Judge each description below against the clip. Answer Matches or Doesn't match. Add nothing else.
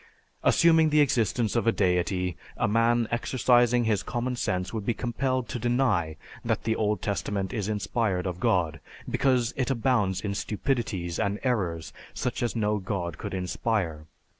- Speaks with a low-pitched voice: Matches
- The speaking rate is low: Doesn't match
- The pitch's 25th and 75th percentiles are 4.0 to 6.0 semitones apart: Matches